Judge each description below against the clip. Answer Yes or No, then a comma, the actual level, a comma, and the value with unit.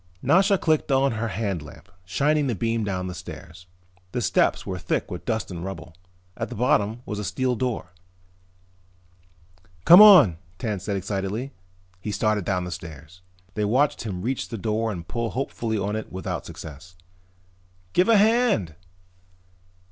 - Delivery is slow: No, average, 160 wpm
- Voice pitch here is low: Yes, low, 110 Hz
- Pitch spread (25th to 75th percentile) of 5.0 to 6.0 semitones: Yes, wide, 5.5 semitones